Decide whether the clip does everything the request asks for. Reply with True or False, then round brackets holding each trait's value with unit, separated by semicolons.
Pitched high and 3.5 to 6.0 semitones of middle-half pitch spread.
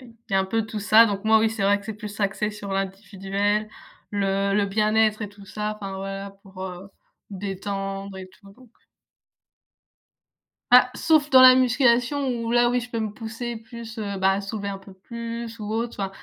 False (210 Hz; 2.8 semitones)